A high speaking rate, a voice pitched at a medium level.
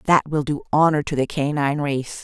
Yes: fast, 215 wpm; medium, 145 Hz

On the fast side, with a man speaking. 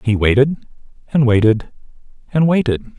No: slow, 120 wpm; male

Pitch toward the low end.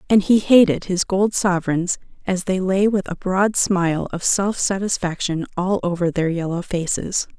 No: medium, 185 Hz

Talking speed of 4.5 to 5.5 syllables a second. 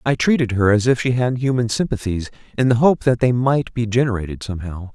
No: 5.9 syllables/s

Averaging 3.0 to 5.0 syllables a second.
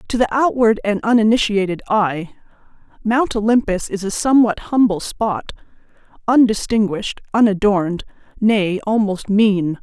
Yes: 4.8 syllables/s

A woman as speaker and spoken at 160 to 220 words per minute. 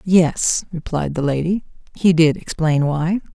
No: female; average, 145 wpm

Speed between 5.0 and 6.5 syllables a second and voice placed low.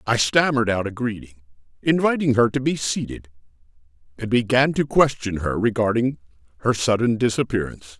Yes: 5.6 syllables/s; low, 115 Hz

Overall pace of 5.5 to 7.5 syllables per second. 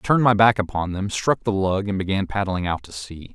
Yes: 5.7 syllables/s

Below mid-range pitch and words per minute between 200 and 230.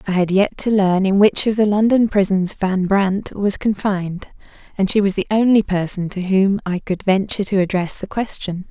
No: high, 195 Hz; fast, 205 wpm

